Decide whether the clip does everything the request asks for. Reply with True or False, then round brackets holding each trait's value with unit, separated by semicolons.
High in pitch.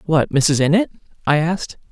False (160 Hz)